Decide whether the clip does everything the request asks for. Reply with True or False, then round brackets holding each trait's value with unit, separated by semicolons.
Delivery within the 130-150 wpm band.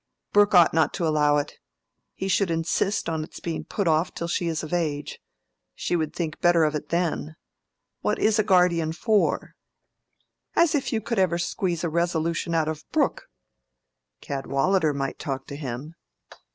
False (170 wpm)